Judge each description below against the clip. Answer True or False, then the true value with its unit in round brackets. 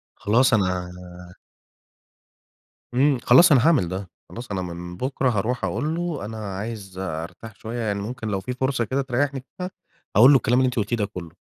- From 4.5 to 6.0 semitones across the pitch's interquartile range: True (5.1 semitones)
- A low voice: True (115 Hz)